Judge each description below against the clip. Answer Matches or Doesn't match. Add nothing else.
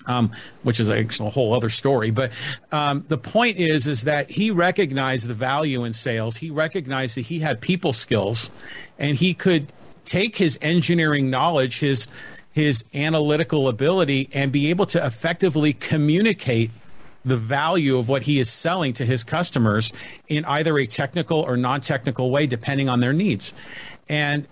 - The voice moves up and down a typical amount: Matches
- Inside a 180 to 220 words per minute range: Doesn't match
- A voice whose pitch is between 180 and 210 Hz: Doesn't match